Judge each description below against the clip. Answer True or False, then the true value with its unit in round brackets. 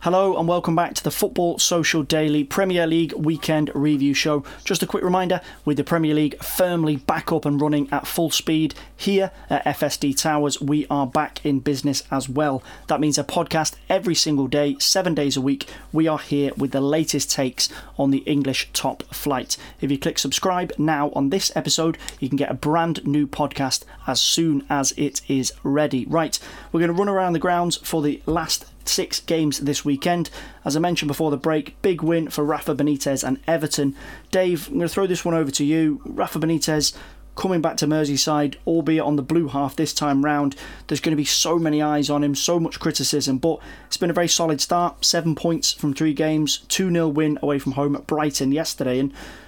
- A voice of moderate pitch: True (150 Hz)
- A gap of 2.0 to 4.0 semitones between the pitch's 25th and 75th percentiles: True (2.6 semitones)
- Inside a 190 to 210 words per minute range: True (205 wpm)